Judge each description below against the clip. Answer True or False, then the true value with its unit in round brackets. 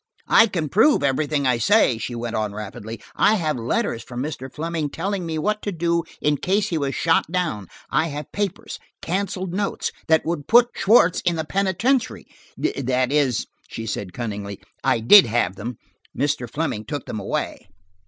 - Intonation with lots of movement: True (7.4 semitones)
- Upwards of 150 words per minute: True (165 wpm)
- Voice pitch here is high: False (150 Hz)